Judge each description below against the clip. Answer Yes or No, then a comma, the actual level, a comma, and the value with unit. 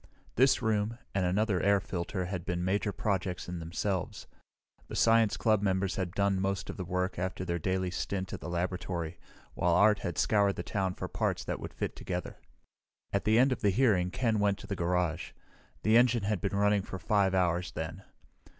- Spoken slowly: No, average, 195 wpm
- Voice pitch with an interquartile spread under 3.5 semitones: Yes, narrow, 2.5 semitones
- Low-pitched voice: Yes, very low, 95 Hz